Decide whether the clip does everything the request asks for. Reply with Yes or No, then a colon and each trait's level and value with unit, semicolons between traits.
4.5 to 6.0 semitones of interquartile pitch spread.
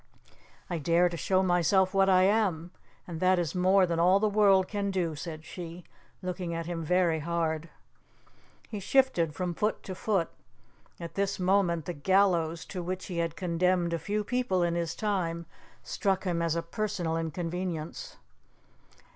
No: narrow, 2.4 semitones